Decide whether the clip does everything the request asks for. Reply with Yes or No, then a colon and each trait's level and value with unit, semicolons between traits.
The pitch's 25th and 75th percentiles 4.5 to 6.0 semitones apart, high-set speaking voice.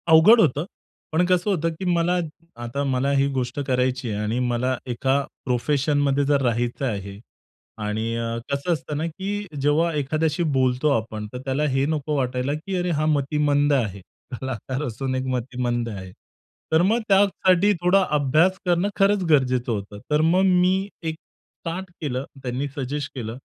No: average, 4.8 semitones; medium, 140 Hz